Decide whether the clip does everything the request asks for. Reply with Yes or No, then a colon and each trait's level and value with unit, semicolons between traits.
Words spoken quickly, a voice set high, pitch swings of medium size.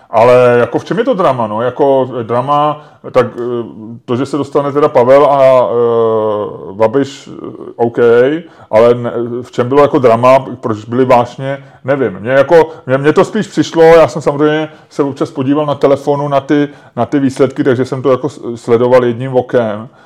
No: fast, 175 wpm; low, 135 Hz; average, 3.6 semitones